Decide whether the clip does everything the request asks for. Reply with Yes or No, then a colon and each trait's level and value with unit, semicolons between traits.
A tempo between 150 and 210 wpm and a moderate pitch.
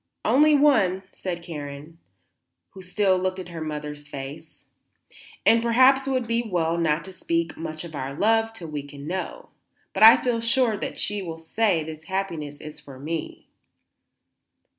Yes: average, 165 wpm; medium, 175 Hz